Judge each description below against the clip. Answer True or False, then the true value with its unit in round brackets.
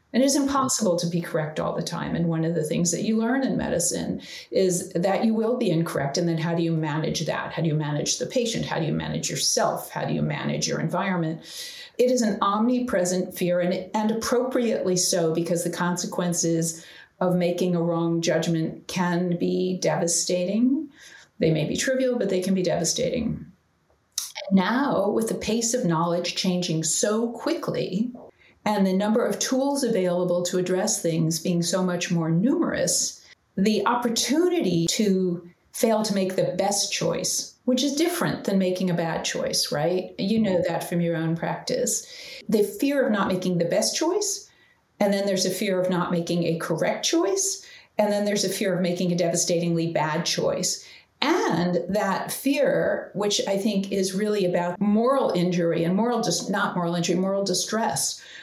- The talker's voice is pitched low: False (185 Hz)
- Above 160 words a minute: True (180 wpm)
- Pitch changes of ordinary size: True (4.7 semitones)